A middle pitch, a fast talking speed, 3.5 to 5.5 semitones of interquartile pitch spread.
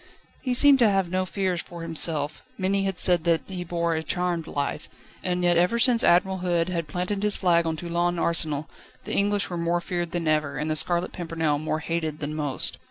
No: medium, 175 Hz; fast, 210 wpm; narrow, 2.4 semitones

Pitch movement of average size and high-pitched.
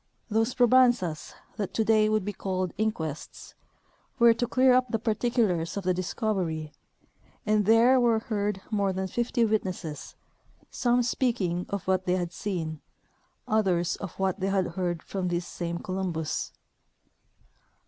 Yes: average, 4.0 semitones; high, 195 Hz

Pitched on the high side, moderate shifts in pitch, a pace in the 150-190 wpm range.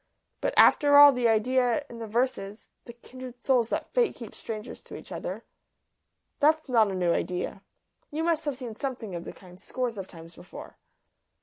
Yes: high, 240 Hz; average, 4.2 semitones; average, 185 wpm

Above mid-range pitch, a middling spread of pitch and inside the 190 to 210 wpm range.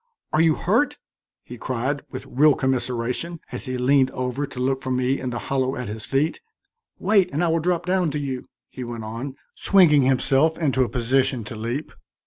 No: low, 135 Hz; average, 3.2 semitones; average, 195 wpm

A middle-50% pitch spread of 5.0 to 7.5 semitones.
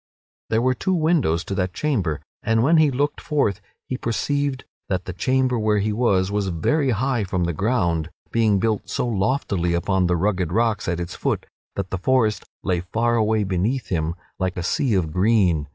Yes: wide, 5.6 semitones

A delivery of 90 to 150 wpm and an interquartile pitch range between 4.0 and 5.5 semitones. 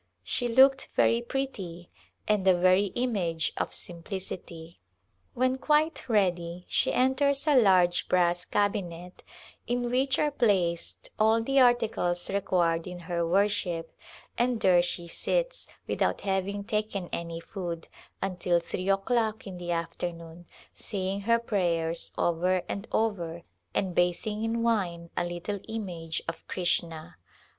Yes: slow, 135 wpm; average, 4.6 semitones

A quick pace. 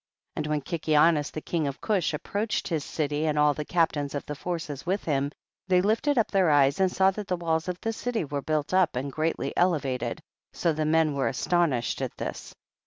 Yes: fast, 210 wpm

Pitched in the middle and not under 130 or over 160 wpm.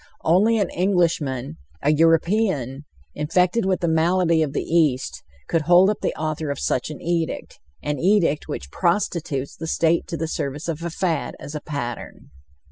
No: medium, 165 Hz; average, 170 wpm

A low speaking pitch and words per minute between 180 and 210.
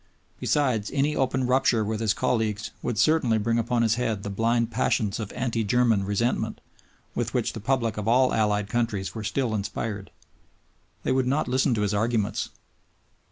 No: low, 115 Hz; average, 170 wpm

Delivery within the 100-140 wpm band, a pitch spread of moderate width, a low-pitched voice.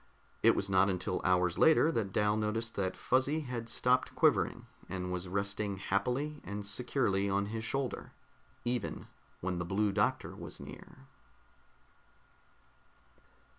Yes: slow, 135 wpm; average, 4.3 semitones; low, 100 Hz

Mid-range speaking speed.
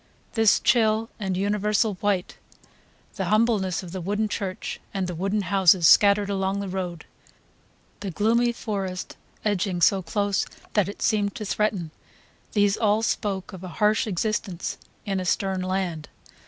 Yes: average, 150 wpm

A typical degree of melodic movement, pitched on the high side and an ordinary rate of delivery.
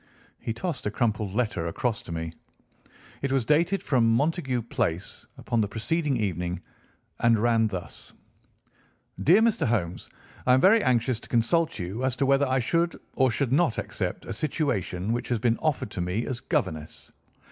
No: average, 4.9 semitones; low, 120 Hz; average, 170 wpm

